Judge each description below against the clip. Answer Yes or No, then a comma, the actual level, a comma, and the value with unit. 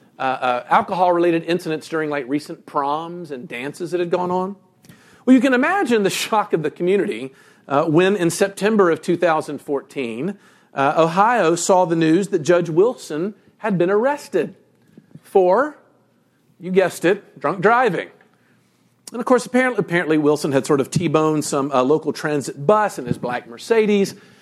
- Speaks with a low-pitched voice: No, medium, 175 Hz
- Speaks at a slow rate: No, average, 160 wpm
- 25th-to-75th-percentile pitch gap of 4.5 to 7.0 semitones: Yes, average, 5.2 semitones